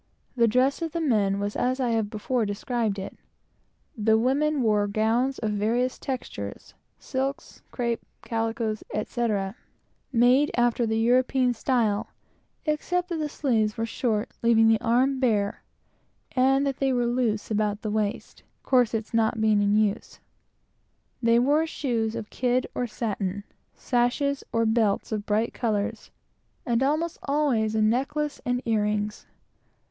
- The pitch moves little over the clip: No, average, 3.2 semitones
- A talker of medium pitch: No, high, 230 Hz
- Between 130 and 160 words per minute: Yes, average, 140 wpm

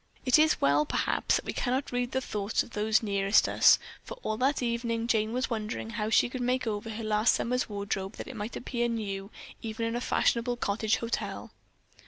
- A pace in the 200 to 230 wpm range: Yes, fast, 205 wpm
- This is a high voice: Yes, high, 230 Hz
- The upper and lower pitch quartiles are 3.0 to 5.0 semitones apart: No, narrow, 2.5 semitones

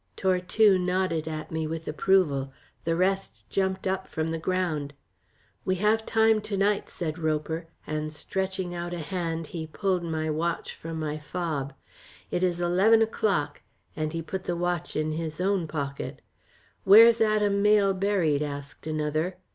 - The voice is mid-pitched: Yes, medium, 175 Hz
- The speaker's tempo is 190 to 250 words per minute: No, average, 155 wpm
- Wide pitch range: No, average, 3.5 semitones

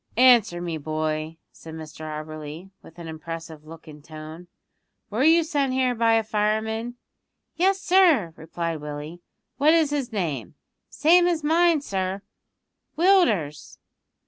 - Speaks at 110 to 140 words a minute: Yes, slow, 135 wpm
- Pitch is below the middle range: No, high, 190 Hz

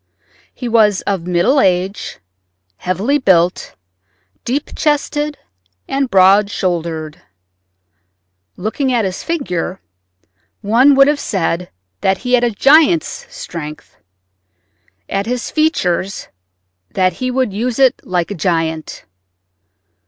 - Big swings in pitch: Yes, wide, 6.7 semitones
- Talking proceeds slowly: Yes, slow, 110 wpm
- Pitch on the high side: Yes, high, 205 Hz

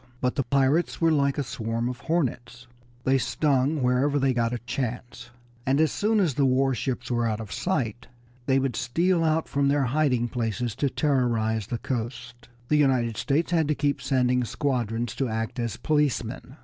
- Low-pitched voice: Yes, low, 130 Hz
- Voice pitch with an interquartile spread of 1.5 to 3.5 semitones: Yes, average, 3.2 semitones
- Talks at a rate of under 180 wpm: No, average, 185 wpm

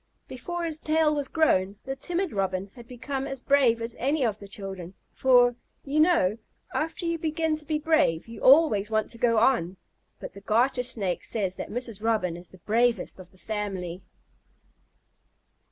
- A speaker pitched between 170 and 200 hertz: No, high, 235 Hz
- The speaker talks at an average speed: Yes, average, 175 wpm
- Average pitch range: No, wide, 6.9 semitones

